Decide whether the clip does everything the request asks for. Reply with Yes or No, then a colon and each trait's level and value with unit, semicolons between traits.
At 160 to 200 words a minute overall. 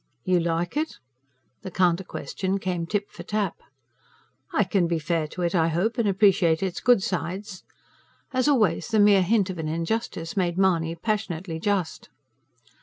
Yes: average, 165 wpm